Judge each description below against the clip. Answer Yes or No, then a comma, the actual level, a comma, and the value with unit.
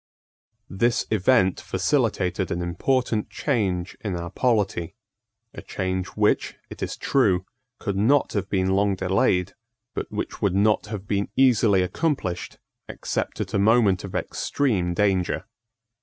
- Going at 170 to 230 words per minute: No, slow, 135 wpm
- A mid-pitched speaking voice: No, low, 100 Hz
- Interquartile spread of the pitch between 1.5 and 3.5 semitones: Yes, average, 3.2 semitones